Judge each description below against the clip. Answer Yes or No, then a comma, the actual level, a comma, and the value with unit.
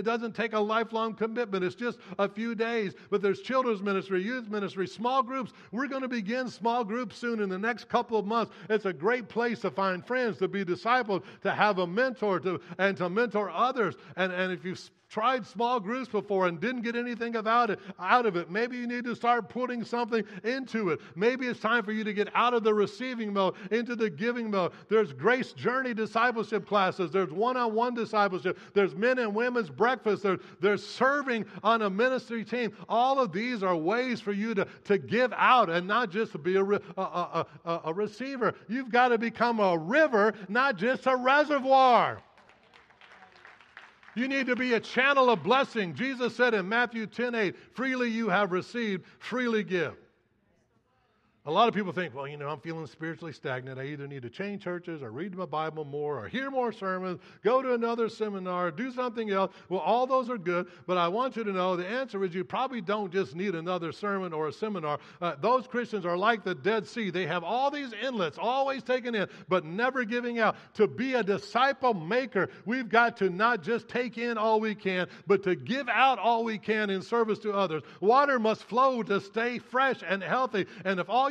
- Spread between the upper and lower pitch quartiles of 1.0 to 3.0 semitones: No, average, 4.2 semitones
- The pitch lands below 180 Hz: No, high, 215 Hz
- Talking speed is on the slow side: No, fast, 205 wpm